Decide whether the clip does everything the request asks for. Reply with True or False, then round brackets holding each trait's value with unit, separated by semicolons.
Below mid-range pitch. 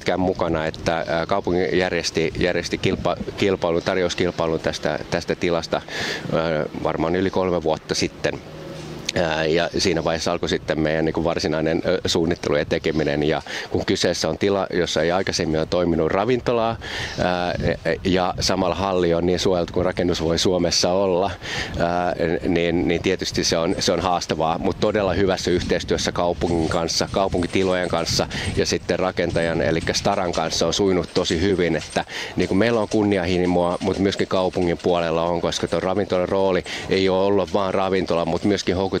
True (90 Hz)